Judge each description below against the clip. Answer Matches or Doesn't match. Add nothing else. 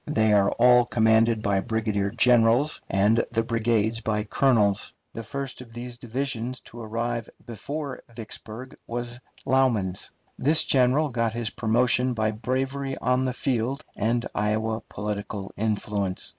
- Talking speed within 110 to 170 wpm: Matches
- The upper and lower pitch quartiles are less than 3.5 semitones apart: Matches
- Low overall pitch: Matches